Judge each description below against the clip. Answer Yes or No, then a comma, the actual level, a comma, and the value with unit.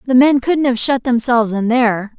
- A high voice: Yes, high, 245 Hz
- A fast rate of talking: Yes, fast, 220 wpm